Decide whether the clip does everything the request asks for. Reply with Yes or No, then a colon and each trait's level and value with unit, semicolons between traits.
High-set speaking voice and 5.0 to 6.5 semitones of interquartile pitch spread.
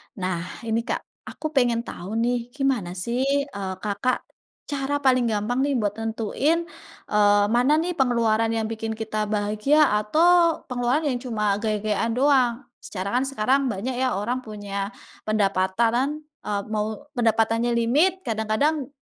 No: high, 230 Hz; average, 3.7 semitones